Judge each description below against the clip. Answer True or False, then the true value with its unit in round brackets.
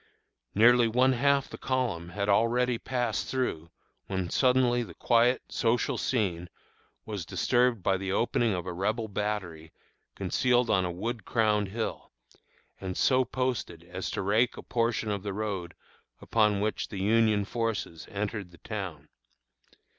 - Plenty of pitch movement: False (4.0 semitones)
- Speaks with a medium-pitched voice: False (105 Hz)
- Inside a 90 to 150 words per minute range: True (145 wpm)